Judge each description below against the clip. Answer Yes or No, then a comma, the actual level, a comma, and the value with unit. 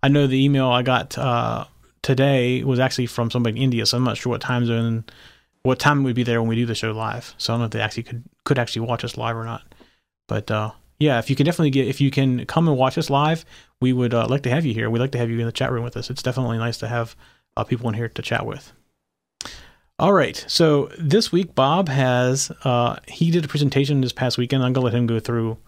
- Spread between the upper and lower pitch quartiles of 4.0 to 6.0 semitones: No, average, 2.8 semitones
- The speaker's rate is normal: No, fast, 270 wpm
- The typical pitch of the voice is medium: No, low, 125 Hz